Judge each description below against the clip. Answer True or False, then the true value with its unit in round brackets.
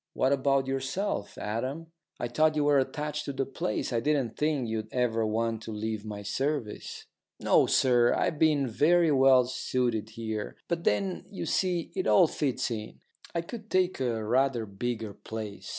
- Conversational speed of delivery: True (170 wpm)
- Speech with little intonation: False (5.1 semitones)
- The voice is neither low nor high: False (130 Hz)